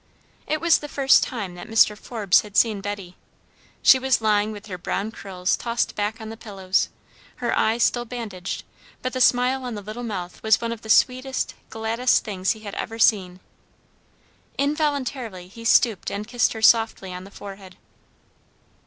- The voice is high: Yes, high, 220 Hz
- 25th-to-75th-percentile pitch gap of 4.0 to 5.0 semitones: No, average, 3.5 semitones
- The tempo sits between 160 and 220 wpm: Yes, average, 175 wpm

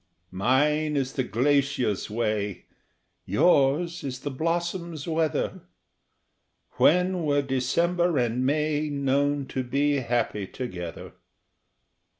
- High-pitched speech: No, medium, 140 Hz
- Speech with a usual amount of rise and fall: Yes, average, 3.8 semitones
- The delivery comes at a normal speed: No, slow, 100 wpm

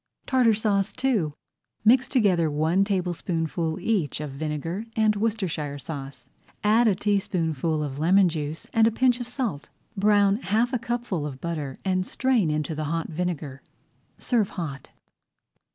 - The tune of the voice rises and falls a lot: Yes, wide, 6.0 semitones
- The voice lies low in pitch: No, medium, 180 Hz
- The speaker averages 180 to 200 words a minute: No, average, 145 wpm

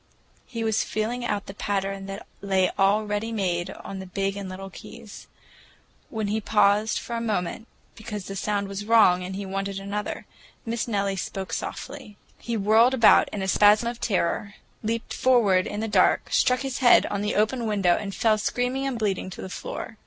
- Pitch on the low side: No, high, 210 Hz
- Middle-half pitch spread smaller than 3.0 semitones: Yes, narrow, 2.6 semitones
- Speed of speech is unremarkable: Yes, average, 190 wpm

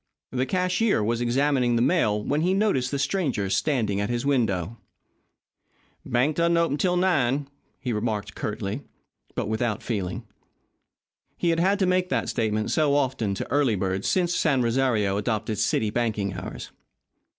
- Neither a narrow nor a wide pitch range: No, wide, 6.3 semitones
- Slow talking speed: No, average, 155 wpm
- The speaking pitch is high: No, low, 125 Hz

